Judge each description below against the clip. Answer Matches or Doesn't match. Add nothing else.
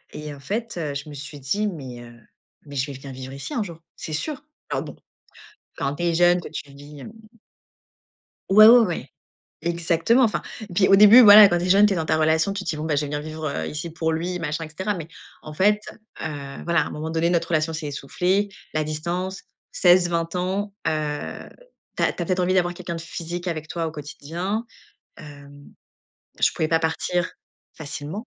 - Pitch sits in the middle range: Matches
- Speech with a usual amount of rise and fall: Matches